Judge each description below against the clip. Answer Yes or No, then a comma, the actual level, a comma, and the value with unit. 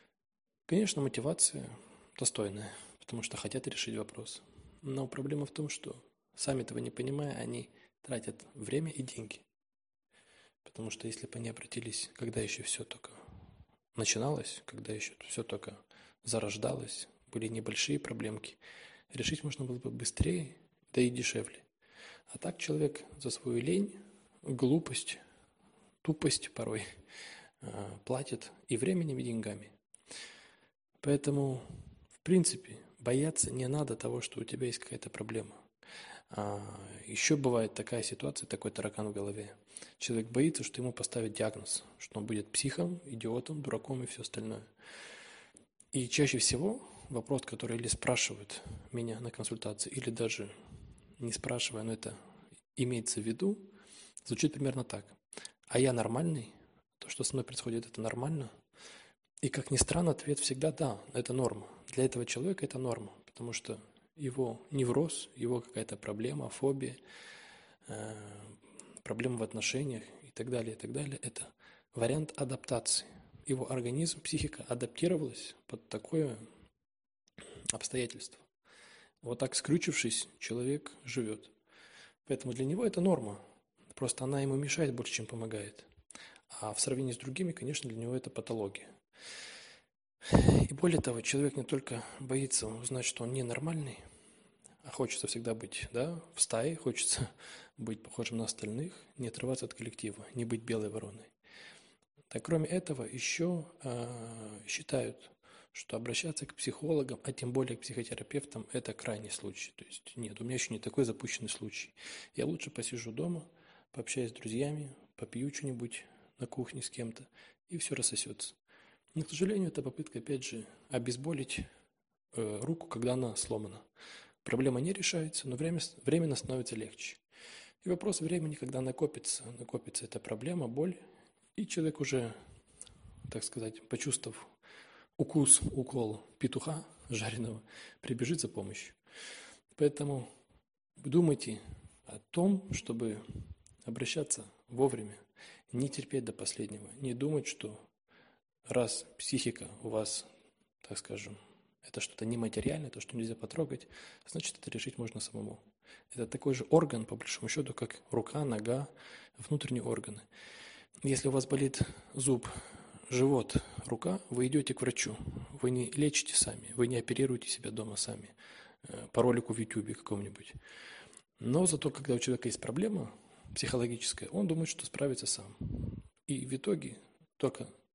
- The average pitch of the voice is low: Yes, low, 125 Hz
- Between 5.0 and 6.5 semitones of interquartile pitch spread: No, average, 4.2 semitones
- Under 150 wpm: Yes, average, 135 wpm